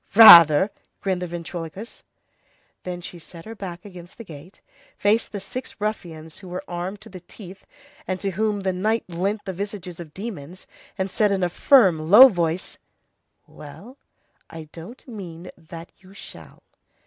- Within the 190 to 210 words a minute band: No, average, 160 wpm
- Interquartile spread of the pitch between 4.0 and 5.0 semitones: No, average, 3.2 semitones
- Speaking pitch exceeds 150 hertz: Yes, medium, 185 Hz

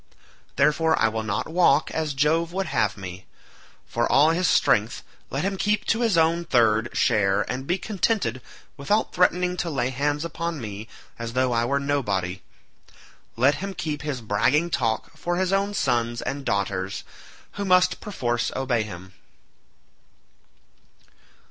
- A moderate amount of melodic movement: No, wide, 6.7 semitones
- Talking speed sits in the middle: Yes, average, 150 wpm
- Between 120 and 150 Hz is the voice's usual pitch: Yes, medium, 140 Hz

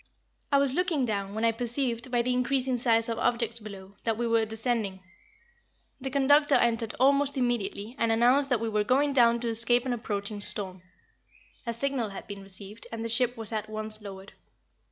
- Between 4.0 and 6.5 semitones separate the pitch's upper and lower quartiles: No, average, 2.7 semitones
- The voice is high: Yes, high, 230 Hz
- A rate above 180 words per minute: Yes, average, 190 wpm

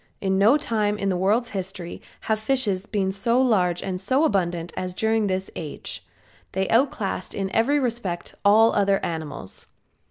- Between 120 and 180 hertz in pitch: No, high, 200 Hz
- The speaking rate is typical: Yes, average, 160 wpm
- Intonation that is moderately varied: Yes, average, 3.4 semitones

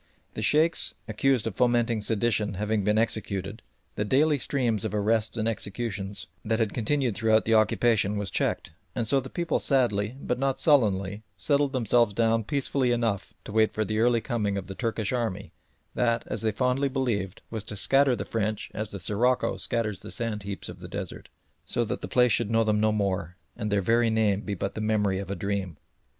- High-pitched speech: No, low, 110 Hz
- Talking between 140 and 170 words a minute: No, average, 200 wpm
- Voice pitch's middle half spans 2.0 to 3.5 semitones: Yes, average, 2.9 semitones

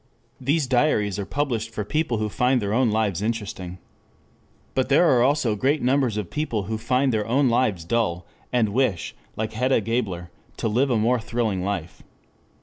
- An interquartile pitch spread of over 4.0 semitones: No, average, 3.7 semitones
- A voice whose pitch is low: Yes, low, 115 Hz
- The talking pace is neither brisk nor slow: Yes, average, 175 wpm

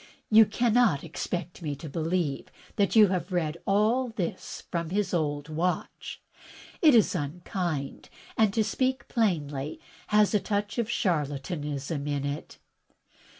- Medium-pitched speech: Yes, medium, 175 Hz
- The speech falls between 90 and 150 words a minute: Yes, slow, 135 wpm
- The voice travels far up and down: Yes, wide, 6.1 semitones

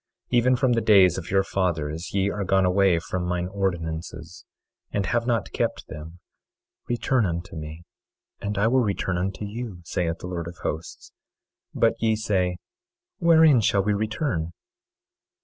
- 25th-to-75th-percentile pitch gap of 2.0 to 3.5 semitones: No, average, 4.0 semitones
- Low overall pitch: Yes, very low, 95 Hz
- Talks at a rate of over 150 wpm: Yes, average, 160 wpm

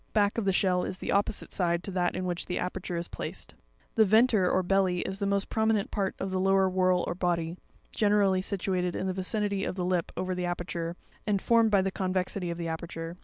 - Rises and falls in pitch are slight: Yes, narrow, 1.9 semitones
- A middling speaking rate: No, fast, 230 wpm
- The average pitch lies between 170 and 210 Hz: Yes, medium, 185 Hz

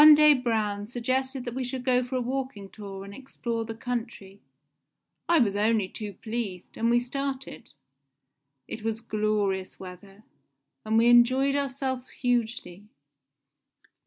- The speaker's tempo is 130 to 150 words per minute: Yes, average, 140 wpm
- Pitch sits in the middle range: No, high, 235 Hz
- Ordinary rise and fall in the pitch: Yes, average, 3.7 semitones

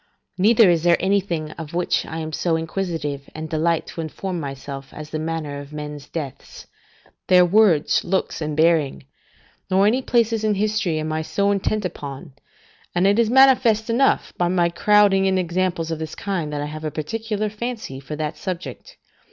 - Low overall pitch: No, medium, 170 Hz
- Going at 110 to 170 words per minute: No, average, 180 wpm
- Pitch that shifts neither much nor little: Yes, average, 4.6 semitones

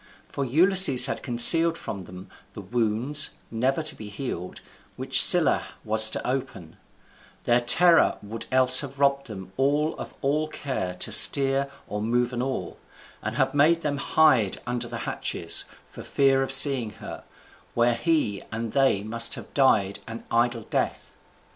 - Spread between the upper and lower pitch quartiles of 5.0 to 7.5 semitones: No, average, 4.1 semitones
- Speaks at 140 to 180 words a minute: Yes, average, 160 wpm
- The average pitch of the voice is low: Yes, low, 125 Hz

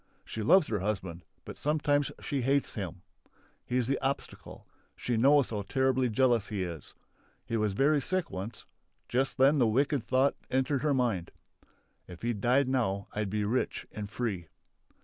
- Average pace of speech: Yes, average, 165 wpm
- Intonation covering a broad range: No, average, 4.7 semitones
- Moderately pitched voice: No, low, 120 Hz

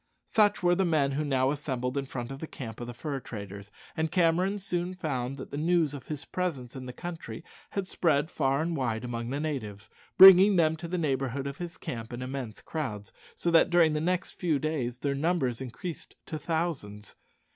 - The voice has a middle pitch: Yes, medium, 145 Hz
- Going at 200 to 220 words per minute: Yes, fast, 205 wpm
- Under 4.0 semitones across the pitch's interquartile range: No, average, 5.1 semitones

